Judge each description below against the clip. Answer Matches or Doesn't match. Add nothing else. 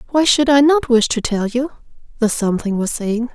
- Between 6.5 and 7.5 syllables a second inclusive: Doesn't match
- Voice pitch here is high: Matches